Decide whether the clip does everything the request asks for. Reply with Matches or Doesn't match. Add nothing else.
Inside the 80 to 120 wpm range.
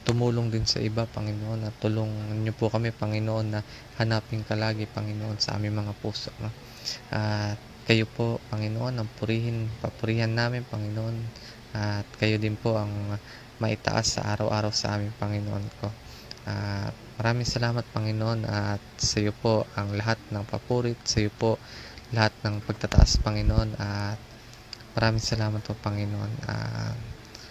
Doesn't match